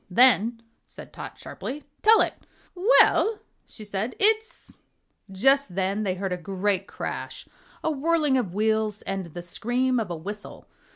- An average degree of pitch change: No, wide, 5.8 semitones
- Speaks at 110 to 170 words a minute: Yes, average, 155 wpm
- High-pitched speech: Yes, high, 215 Hz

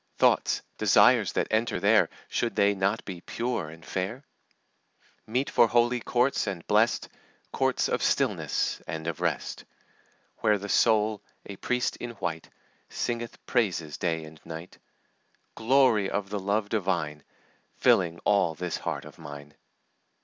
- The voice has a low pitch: Yes, low, 100 Hz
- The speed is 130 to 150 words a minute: Yes, average, 140 wpm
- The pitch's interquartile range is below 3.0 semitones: No, wide, 5.6 semitones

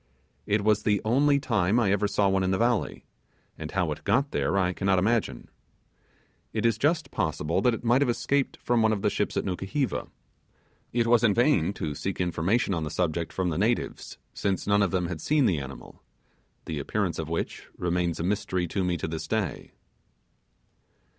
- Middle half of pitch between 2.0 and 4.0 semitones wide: No, average, 4.9 semitones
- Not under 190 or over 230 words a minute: Yes, average, 195 wpm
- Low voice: Yes, low, 100 Hz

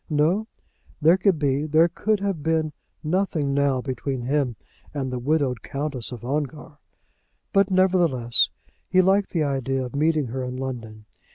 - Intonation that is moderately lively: Yes, average, 4.0 semitones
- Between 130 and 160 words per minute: Yes, average, 155 wpm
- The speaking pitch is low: No, medium, 145 Hz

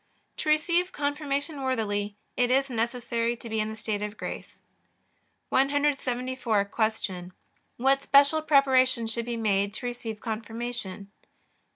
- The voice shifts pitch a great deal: No, average, 4.0 semitones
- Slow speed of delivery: Yes, slow, 130 wpm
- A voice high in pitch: Yes, high, 240 Hz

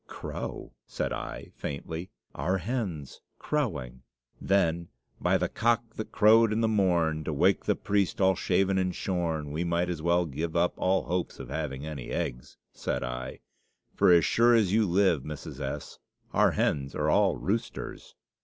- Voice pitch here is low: Yes, very low, 90 Hz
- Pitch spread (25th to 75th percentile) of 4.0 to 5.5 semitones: Yes, average, 4.3 semitones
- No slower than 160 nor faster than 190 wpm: Yes, average, 165 wpm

